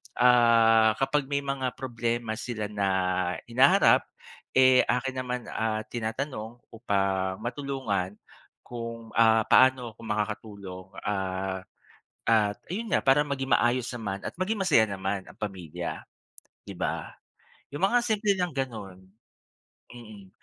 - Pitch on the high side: No, low, 115 Hz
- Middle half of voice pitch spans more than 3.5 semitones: Yes, average, 4.2 semitones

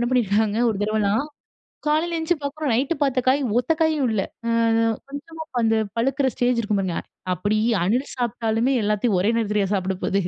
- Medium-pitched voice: No, high, 230 Hz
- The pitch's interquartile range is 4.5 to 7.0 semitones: Yes, average, 4.8 semitones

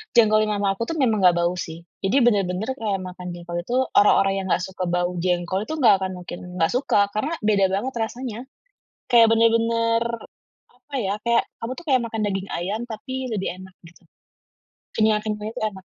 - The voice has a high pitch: Yes, high, 210 Hz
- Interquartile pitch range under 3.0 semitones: No, average, 3.6 semitones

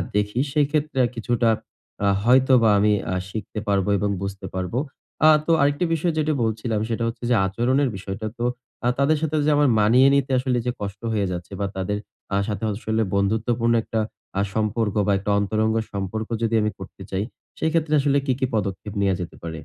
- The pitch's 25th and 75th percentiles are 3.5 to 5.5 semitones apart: Yes, average, 4.4 semitones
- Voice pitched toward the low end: Yes, low, 110 Hz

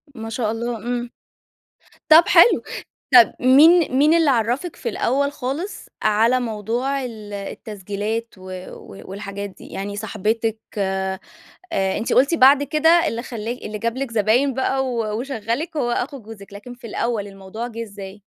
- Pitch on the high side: Yes, high, 230 Hz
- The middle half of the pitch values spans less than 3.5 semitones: No, average, 3.9 semitones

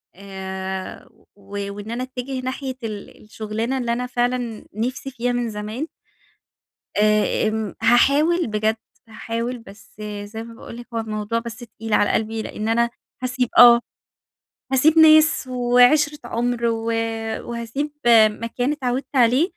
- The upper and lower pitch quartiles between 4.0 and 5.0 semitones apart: No, average, 2.8 semitones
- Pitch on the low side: No, high, 235 Hz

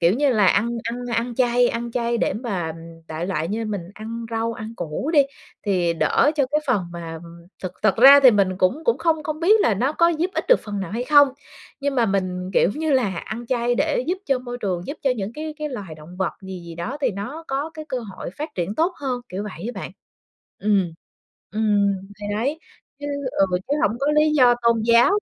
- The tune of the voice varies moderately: No, wide, 6.2 semitones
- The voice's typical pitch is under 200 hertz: No, high, 230 Hz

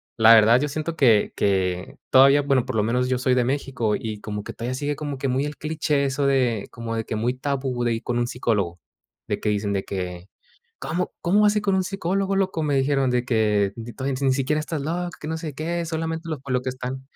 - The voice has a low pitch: Yes, low, 130 Hz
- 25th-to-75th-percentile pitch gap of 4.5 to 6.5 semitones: Yes, average, 5.0 semitones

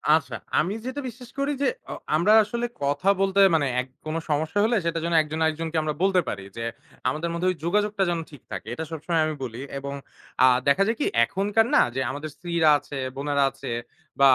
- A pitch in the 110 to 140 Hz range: No, medium, 165 Hz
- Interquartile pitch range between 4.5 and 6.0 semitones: Yes, average, 5.1 semitones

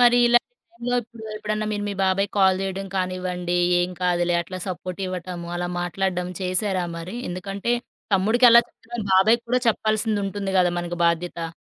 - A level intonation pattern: No, average, 3.2 semitones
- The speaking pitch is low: No, high, 190 Hz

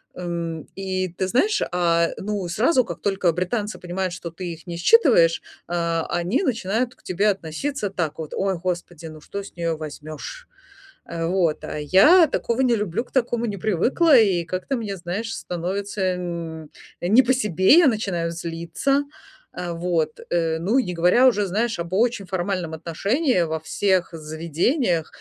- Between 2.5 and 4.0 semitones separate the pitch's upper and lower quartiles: No, average, 4.6 semitones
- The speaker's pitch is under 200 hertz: Yes, medium, 185 Hz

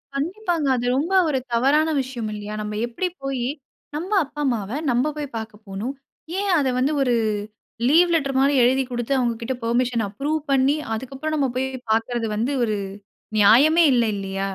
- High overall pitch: Yes, very high, 260 Hz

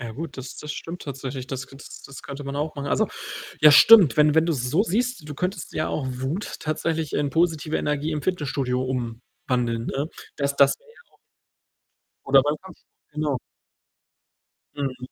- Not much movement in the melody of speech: No, average, 3.2 semitones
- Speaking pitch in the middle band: Yes, medium, 145 Hz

